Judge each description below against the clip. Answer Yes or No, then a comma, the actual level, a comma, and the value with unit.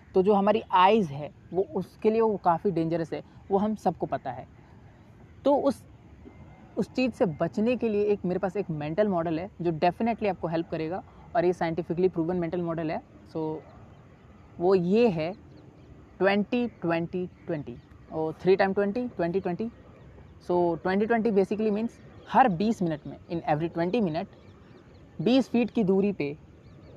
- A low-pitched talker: No, medium, 185 Hz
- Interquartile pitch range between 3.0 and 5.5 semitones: Yes, average, 4.0 semitones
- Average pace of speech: Yes, average, 170 wpm